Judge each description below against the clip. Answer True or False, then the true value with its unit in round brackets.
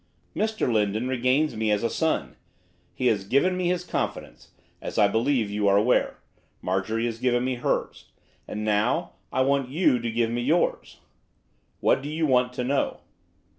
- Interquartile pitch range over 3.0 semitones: True (4.3 semitones)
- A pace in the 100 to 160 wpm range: False (170 wpm)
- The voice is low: True (125 Hz)